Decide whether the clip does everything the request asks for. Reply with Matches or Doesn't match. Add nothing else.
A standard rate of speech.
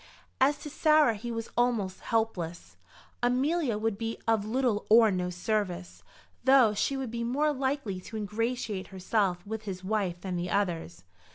Matches